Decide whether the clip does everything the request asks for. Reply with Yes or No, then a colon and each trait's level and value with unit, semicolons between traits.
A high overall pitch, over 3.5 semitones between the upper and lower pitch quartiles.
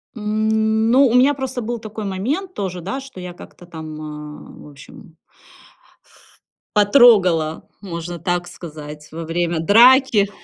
Yes: high, 195 Hz; wide, 5.5 semitones